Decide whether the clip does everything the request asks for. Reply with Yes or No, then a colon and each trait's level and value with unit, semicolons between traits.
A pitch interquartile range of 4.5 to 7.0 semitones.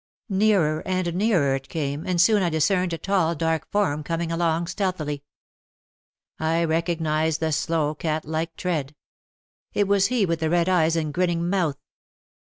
No: narrow, 2.6 semitones